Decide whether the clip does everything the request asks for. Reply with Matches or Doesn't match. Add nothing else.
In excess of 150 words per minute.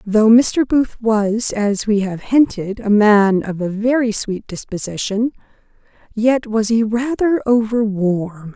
Doesn't match